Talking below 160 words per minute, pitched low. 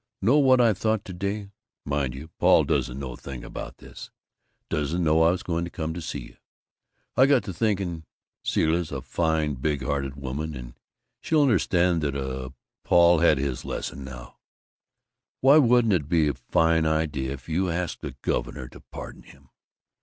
No: average, 175 wpm; very low, 80 Hz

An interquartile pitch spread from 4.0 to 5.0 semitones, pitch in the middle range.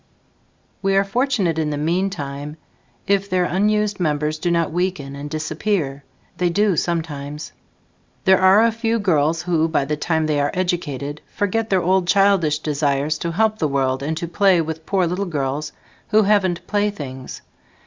Yes: average, 4.5 semitones; medium, 170 Hz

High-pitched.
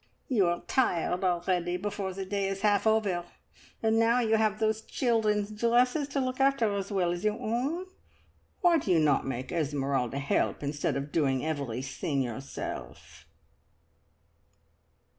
Yes: high, 195 Hz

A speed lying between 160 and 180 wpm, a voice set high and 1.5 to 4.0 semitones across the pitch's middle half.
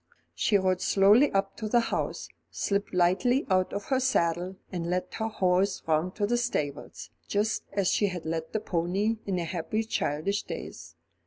Yes: average, 175 wpm; high, 195 Hz; average, 3.4 semitones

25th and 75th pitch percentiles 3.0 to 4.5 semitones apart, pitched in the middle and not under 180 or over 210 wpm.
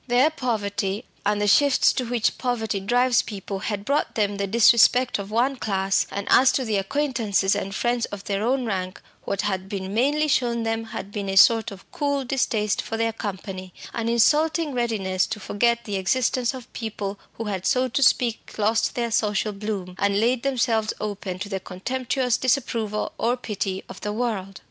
No: average, 3.6 semitones; high, 220 Hz; average, 185 wpm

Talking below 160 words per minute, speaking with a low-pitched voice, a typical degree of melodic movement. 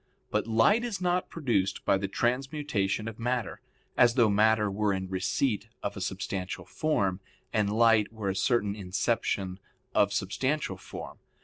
Yes: average, 150 wpm; low, 110 Hz; average, 4.0 semitones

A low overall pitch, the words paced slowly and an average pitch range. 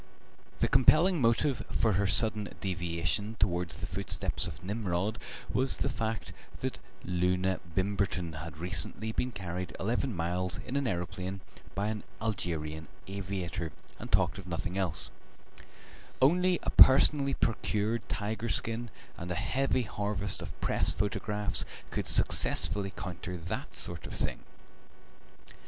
Yes: low, 100 Hz; slow, 130 wpm; average, 4.0 semitones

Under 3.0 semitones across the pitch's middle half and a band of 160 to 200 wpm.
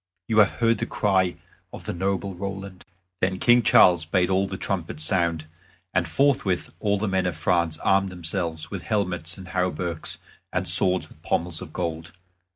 Yes: narrow, 2.4 semitones; average, 170 wpm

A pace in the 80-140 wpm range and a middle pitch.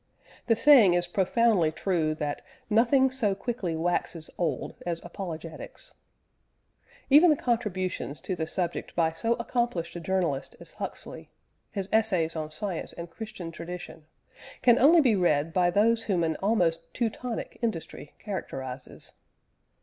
Yes: slow, 135 wpm; medium, 180 Hz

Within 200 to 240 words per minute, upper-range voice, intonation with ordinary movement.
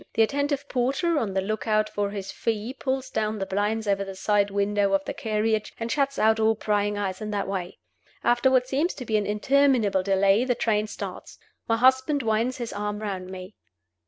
Yes: fast, 205 wpm; high, 215 Hz; average, 3.7 semitones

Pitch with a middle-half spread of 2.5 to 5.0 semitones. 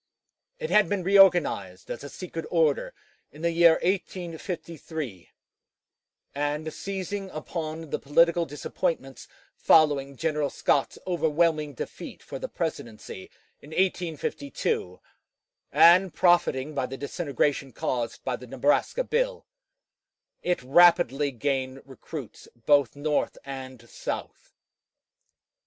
Yes: average, 4.2 semitones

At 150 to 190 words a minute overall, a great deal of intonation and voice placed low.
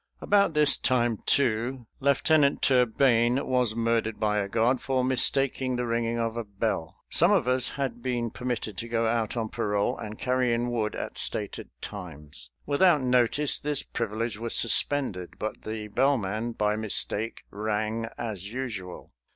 No: average, 155 wpm; average, 3.0 semitones; low, 115 Hz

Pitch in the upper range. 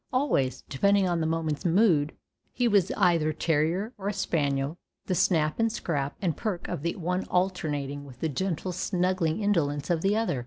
No: medium, 170 Hz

